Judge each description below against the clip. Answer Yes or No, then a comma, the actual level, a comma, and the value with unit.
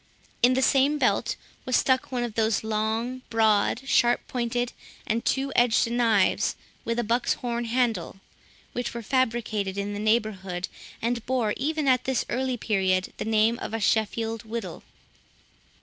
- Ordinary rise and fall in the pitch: No, narrow, 2.3 semitones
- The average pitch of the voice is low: No, high, 230 Hz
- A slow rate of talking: No, average, 155 wpm